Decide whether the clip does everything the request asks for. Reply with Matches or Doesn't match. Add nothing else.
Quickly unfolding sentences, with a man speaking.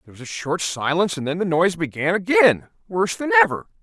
Matches